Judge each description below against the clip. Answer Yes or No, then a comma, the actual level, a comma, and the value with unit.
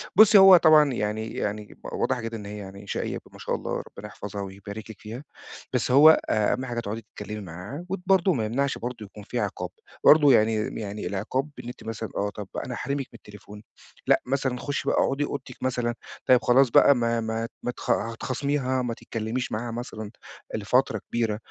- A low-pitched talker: Yes, low, 115 Hz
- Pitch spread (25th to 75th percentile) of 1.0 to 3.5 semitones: No, average, 3.9 semitones